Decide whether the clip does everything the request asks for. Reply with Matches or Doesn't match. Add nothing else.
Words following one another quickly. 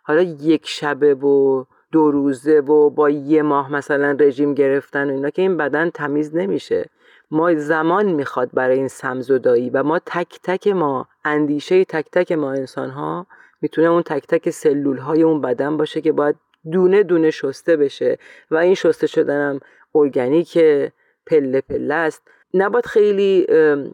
Matches